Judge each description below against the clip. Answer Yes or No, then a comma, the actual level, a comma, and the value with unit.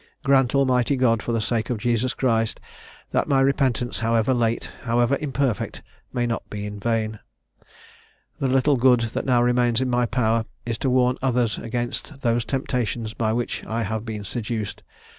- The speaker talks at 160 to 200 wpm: Yes, average, 170 wpm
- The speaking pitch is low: Yes, low, 120 Hz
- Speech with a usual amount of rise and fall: No, narrow, 2.1 semitones